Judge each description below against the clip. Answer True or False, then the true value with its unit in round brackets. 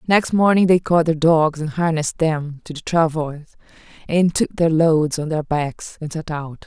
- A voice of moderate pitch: True (160 Hz)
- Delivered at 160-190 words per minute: False (200 wpm)